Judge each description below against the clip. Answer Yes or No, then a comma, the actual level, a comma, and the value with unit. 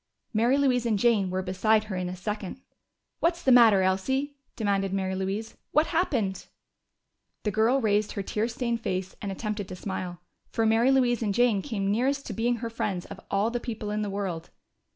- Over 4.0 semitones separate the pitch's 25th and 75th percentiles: No, average, 3.7 semitones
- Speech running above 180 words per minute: Yes, average, 195 wpm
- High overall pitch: Yes, high, 215 Hz